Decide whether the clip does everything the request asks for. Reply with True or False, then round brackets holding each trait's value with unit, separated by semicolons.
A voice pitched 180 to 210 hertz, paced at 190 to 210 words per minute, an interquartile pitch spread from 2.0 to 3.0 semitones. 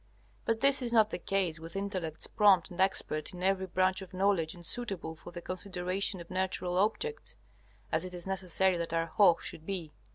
True (185 Hz; 195 wpm; 2.4 semitones)